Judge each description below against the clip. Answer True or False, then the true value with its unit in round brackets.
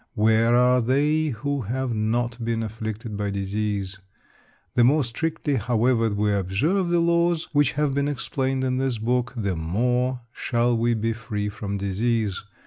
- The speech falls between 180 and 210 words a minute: False (155 wpm)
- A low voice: True (120 Hz)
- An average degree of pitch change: True (3.6 semitones)